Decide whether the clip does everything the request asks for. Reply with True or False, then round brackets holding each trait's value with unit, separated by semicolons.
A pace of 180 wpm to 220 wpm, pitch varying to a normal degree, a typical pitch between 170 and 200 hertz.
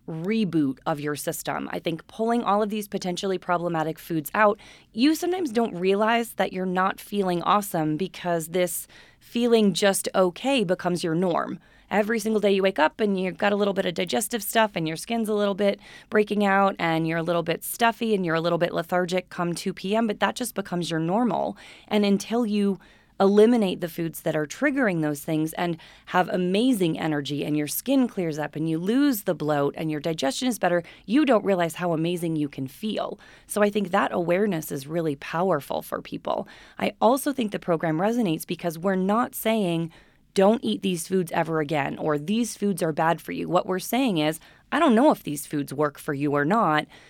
True (205 wpm; 4.7 semitones; 185 Hz)